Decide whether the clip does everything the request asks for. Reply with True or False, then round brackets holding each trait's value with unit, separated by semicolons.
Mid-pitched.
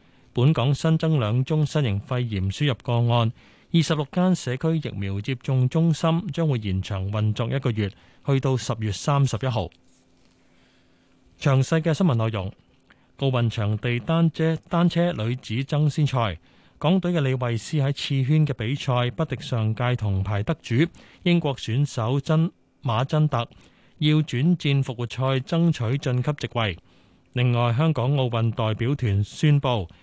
False (130 Hz)